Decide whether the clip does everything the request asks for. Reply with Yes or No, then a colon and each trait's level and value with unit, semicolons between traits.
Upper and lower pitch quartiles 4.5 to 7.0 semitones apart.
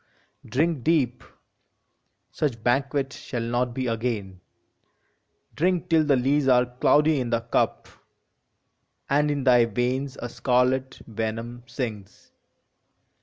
No: average, 3.0 semitones